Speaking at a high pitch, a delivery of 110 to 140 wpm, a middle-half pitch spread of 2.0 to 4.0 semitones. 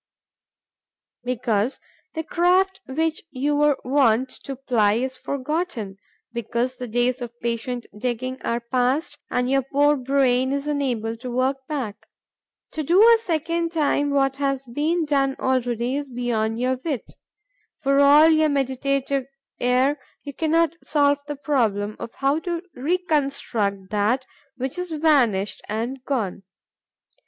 Yes: very high, 270 Hz; slow, 135 wpm; average, 3.3 semitones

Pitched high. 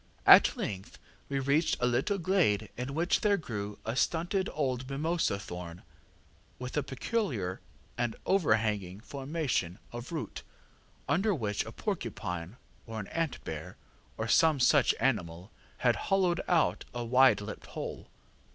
No: low, 125 Hz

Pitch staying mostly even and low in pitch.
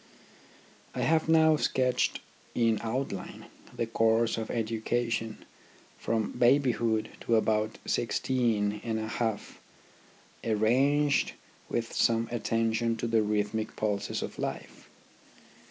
Yes: narrow, 1.7 semitones; low, 115 Hz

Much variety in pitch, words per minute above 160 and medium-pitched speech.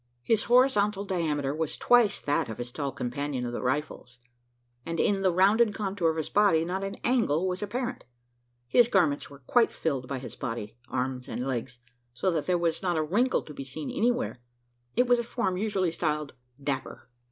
Yes: wide, 6.8 semitones; average, 190 wpm; medium, 165 Hz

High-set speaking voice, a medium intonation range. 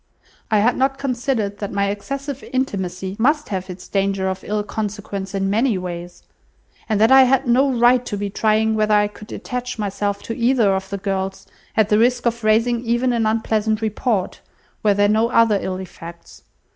Yes: high, 215 Hz; average, 3.3 semitones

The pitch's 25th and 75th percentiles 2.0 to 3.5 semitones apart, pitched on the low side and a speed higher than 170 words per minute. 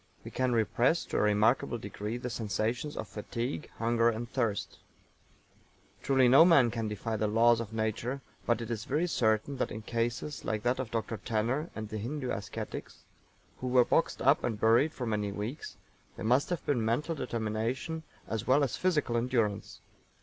Yes: average, 3.0 semitones; low, 115 Hz; average, 180 wpm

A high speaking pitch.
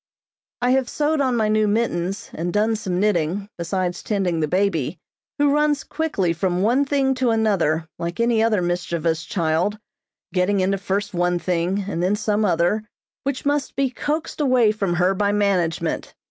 Yes: high, 200 Hz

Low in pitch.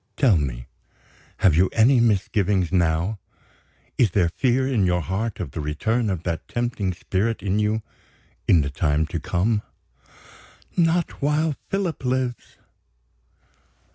Yes: low, 105 Hz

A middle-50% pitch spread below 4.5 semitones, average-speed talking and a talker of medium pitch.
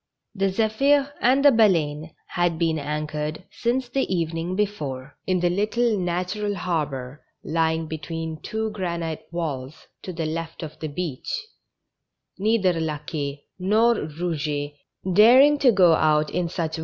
No: average, 5.2 semitones; average, 150 wpm; medium, 170 Hz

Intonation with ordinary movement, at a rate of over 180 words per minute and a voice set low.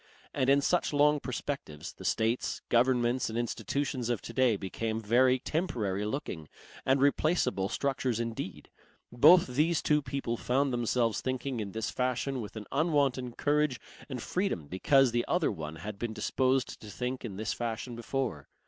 No: average, 3.7 semitones; average, 160 wpm; low, 125 Hz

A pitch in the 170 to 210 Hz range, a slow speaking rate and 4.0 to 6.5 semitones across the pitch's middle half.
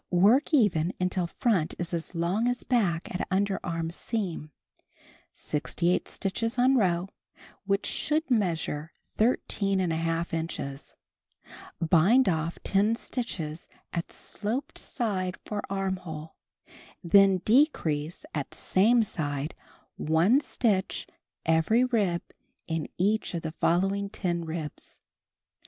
Yes: medium, 185 Hz; slow, 105 wpm; average, 4.9 semitones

